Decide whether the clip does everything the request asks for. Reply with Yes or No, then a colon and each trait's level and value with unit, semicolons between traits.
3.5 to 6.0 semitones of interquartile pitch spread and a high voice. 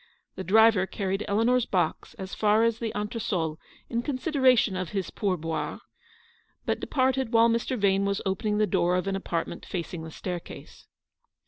Yes: average, 3.8 semitones; high, 205 Hz